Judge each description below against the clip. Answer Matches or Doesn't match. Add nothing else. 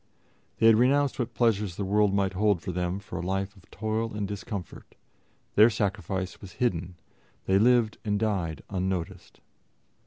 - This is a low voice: Matches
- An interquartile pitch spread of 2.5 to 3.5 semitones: Matches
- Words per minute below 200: Matches